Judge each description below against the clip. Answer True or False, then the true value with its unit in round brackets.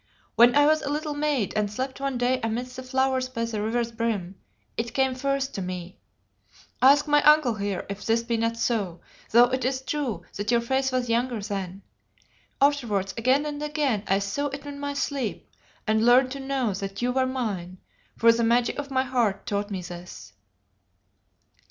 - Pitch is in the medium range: False (245 Hz)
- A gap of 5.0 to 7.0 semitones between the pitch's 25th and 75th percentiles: False (4.1 semitones)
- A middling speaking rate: True (190 wpm)